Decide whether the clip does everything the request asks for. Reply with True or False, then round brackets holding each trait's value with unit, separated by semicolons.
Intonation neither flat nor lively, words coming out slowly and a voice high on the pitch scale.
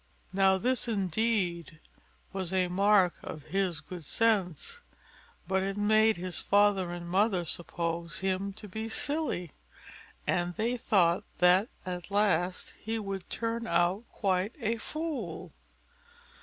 True (3.6 semitones; 130 wpm; 195 Hz)